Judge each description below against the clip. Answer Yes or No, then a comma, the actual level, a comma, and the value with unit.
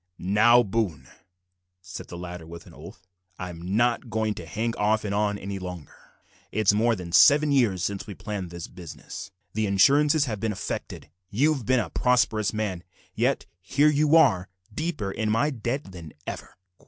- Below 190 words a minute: Yes, average, 170 wpm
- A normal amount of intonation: Yes, average, 4.7 semitones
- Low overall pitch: Yes, low, 105 Hz